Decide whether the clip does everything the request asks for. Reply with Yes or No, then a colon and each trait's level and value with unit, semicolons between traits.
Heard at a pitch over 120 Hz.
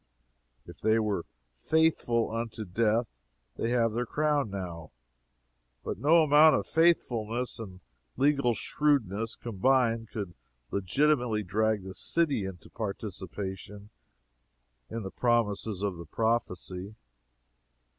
No: low, 110 Hz